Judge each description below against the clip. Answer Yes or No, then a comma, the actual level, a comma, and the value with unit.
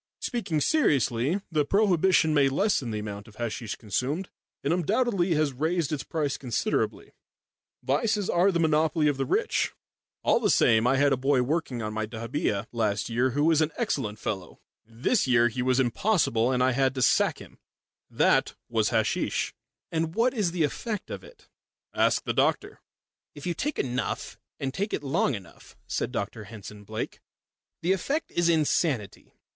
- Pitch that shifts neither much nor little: No, wide, 6.4 semitones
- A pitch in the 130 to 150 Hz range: Yes, medium, 140 Hz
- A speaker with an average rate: Yes, average, 170 wpm